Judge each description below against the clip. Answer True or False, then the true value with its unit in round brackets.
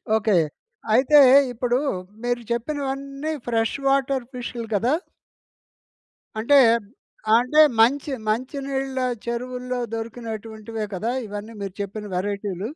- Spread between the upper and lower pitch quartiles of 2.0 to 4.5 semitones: True (3.4 semitones)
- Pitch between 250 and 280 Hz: False (240 Hz)